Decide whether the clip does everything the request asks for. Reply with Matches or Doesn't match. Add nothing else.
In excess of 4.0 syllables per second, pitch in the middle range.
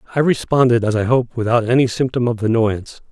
Doesn't match